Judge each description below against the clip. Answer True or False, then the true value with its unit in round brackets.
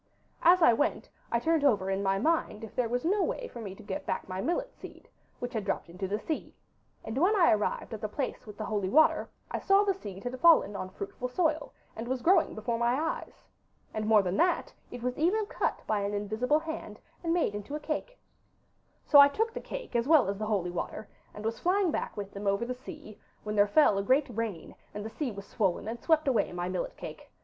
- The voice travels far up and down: True (7.5 semitones)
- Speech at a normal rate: False (235 wpm)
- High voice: True (235 Hz)